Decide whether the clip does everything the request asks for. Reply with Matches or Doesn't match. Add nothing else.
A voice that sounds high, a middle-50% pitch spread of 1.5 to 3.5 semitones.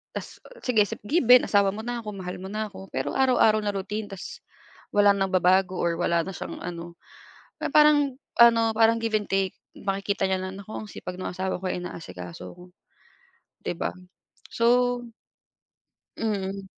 Matches